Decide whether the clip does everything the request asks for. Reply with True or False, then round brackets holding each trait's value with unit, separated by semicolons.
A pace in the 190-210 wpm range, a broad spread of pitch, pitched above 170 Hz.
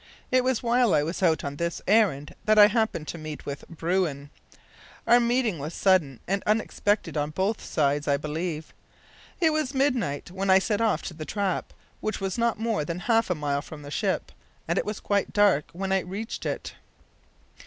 True (195 wpm; 6.2 semitones; 190 Hz)